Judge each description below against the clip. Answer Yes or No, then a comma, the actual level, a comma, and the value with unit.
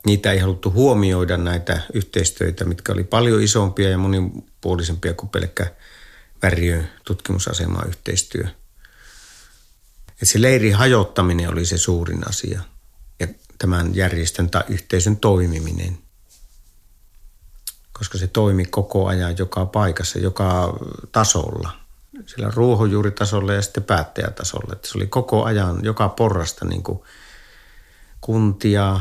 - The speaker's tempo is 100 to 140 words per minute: Yes, average, 115 wpm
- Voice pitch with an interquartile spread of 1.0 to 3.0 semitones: Yes, average, 2.7 semitones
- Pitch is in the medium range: No, very low, 95 Hz